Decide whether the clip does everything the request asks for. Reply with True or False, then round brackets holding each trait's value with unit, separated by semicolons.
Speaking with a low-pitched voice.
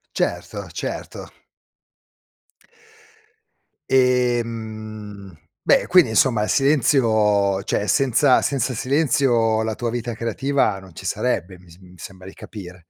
True (110 Hz)